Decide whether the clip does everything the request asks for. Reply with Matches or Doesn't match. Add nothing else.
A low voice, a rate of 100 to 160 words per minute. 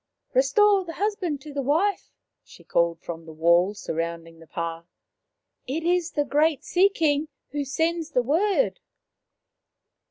Doesn't match